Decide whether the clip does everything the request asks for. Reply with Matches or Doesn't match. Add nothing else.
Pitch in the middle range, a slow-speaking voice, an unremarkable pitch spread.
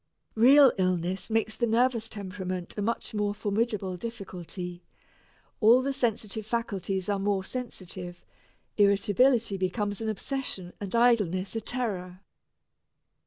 Doesn't match